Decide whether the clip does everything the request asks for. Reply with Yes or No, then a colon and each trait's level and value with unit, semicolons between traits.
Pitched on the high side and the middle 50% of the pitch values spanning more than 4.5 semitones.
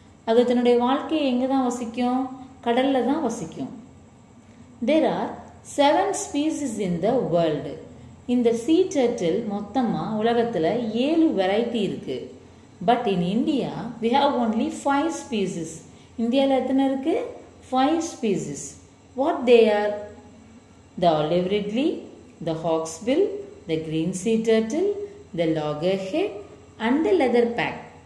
Yes: high, 240 Hz; wide, 5.5 semitones